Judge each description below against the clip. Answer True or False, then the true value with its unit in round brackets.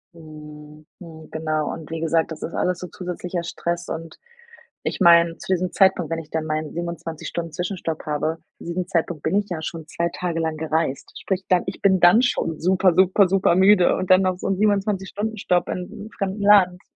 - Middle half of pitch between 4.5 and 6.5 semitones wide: False (2.7 semitones)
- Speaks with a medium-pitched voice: True (175 Hz)